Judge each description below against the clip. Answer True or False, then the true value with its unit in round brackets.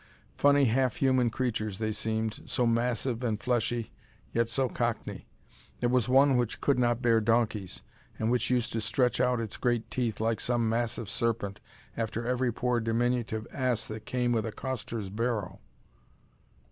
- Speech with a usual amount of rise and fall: False (1.9 semitones)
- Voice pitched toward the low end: True (115 Hz)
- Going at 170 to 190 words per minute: False (160 wpm)